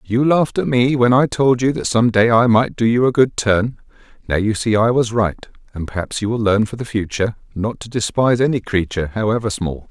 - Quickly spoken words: Yes, fast, 235 wpm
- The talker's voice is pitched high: No, low, 115 Hz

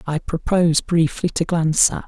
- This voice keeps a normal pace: Yes, average, 175 wpm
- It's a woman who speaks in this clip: No, male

